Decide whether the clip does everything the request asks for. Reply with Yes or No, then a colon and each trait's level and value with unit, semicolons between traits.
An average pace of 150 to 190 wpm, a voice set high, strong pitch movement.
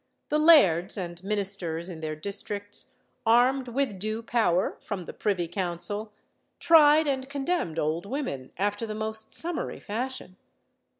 No: slow, 135 wpm; high, 210 Hz; wide, 6.4 semitones